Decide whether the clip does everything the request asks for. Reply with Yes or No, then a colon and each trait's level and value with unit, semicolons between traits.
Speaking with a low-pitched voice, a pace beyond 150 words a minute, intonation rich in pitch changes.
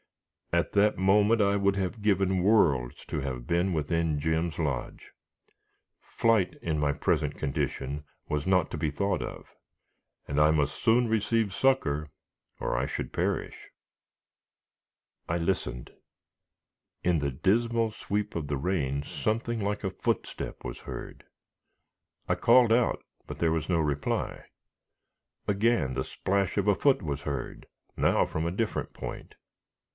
No: very low, 90 Hz; average, 140 wpm; wide, 5.7 semitones